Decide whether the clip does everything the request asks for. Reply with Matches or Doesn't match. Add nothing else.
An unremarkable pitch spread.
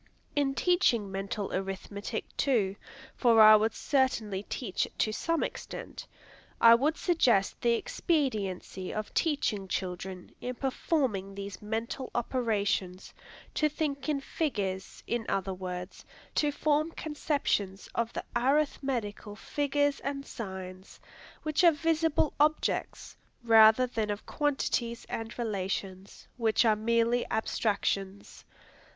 Doesn't match